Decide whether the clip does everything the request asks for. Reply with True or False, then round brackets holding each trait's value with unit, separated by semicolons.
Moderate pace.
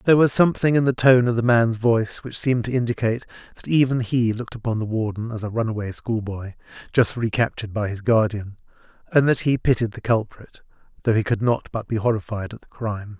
False (210 wpm)